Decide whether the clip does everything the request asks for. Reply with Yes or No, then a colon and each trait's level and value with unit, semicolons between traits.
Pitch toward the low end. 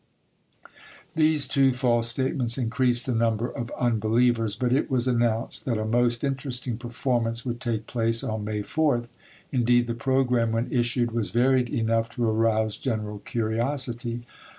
Yes: low, 120 Hz